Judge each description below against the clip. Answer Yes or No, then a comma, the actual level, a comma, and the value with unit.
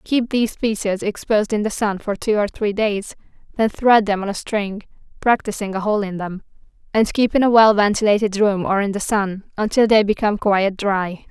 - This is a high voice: Yes, high, 205 Hz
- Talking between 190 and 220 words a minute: Yes, fast, 205 wpm